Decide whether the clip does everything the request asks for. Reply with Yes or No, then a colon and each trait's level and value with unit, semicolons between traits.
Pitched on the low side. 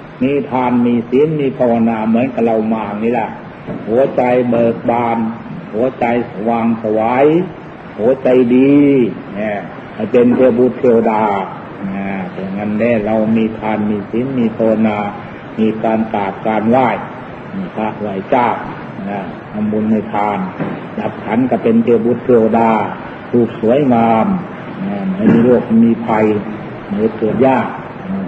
Yes: low, 115 Hz